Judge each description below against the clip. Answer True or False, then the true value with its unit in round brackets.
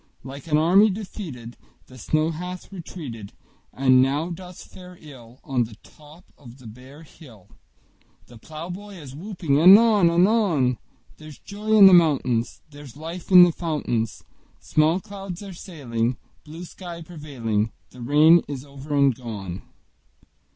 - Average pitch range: False (5.7 semitones)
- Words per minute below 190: True (145 wpm)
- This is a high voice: False (155 Hz)